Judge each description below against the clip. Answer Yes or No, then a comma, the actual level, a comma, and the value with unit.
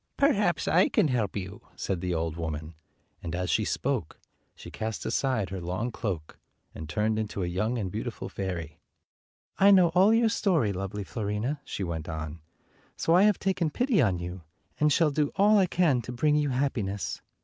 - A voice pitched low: Yes, low, 110 Hz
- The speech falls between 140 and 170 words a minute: No, average, 195 wpm